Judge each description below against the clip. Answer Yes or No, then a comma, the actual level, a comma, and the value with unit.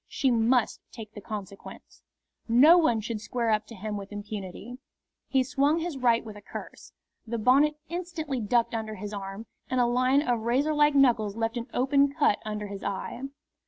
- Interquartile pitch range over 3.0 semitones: Yes, average, 4.2 semitones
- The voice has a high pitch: Yes, high, 235 Hz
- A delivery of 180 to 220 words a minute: Yes, average, 185 wpm